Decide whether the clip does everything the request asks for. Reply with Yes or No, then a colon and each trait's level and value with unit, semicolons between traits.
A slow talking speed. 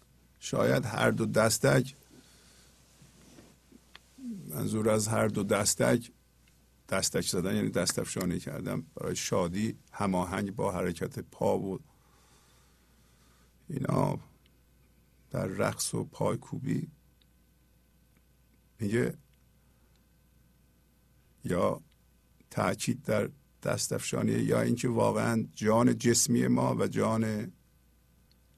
Yes: slow, 85 wpm